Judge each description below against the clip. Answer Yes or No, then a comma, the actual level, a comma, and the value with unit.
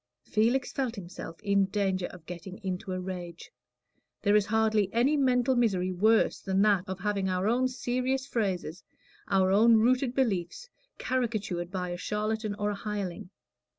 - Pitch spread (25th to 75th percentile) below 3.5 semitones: No, average, 3.9 semitones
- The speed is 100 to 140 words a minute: No, average, 155 wpm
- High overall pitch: Yes, high, 205 Hz